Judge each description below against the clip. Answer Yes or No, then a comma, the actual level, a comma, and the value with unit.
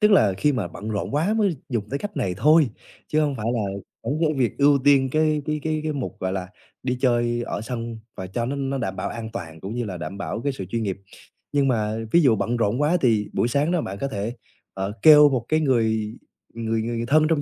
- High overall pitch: No, low, 120 Hz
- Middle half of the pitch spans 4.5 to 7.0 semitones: Yes, wide, 5.4 semitones